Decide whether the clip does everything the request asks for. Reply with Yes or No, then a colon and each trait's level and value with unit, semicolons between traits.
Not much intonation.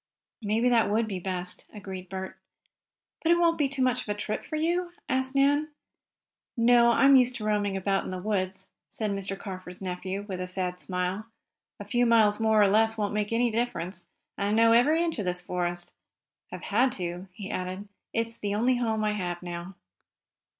No: average, 4.1 semitones